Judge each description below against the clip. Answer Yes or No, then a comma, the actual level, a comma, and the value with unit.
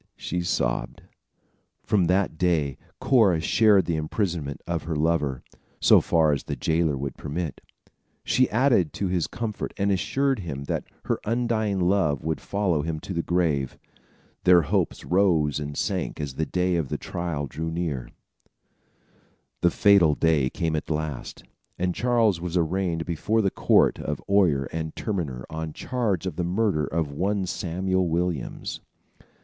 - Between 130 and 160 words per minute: Yes, average, 155 wpm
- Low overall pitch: Yes, very low, 85 Hz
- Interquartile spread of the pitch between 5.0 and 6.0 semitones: No, average, 4.0 semitones